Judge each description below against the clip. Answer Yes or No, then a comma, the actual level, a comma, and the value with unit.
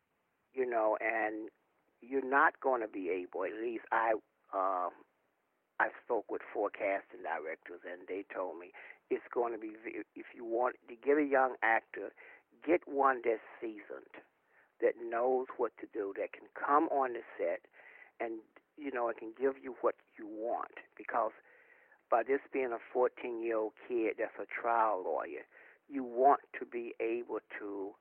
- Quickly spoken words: No, average, 170 wpm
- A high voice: Yes, very high, 365 Hz